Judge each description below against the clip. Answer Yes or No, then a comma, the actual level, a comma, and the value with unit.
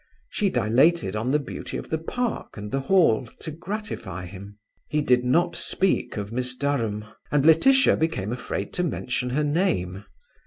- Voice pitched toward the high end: No, low, 135 Hz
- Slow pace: No, average, 165 wpm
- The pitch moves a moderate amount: No, wide, 7.4 semitones